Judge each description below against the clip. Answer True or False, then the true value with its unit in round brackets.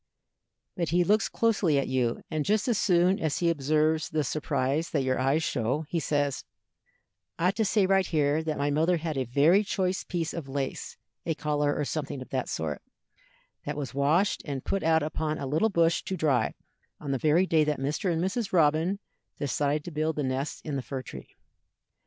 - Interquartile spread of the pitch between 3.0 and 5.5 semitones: True (3.5 semitones)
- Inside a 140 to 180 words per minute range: False (200 wpm)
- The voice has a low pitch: False (155 Hz)